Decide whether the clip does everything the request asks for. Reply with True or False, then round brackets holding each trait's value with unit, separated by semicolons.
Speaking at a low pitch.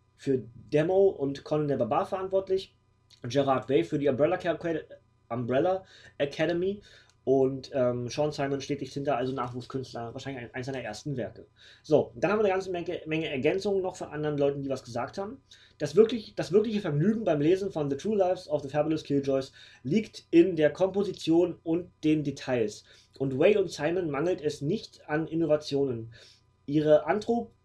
False (150 Hz)